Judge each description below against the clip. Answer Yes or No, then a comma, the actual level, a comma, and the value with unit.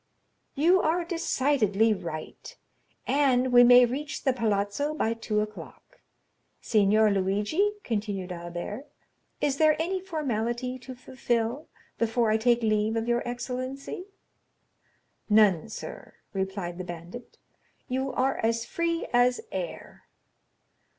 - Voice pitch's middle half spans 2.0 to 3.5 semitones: No, average, 4.3 semitones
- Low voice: No, high, 240 Hz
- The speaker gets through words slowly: Yes, slow, 115 wpm